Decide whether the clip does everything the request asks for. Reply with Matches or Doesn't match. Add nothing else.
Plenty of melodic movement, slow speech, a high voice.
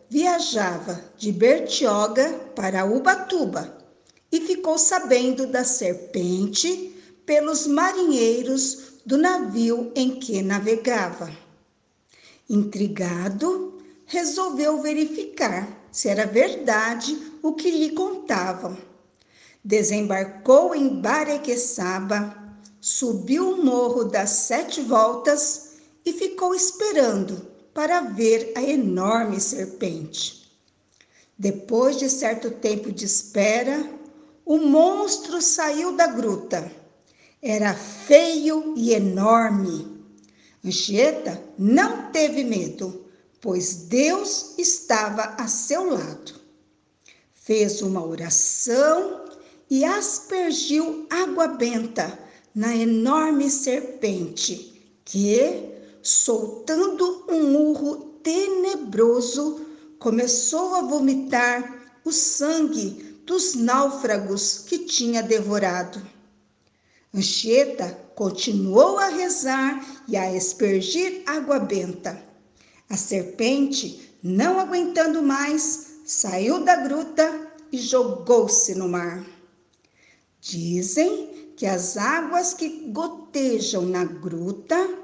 Matches